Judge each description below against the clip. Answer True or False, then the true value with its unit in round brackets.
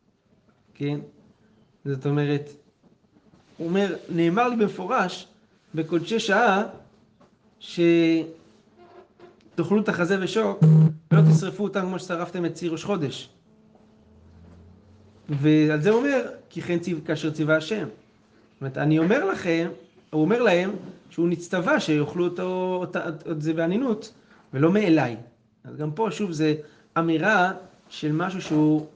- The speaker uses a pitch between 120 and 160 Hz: False (170 Hz)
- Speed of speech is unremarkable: True (120 wpm)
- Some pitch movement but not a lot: True (3.6 semitones)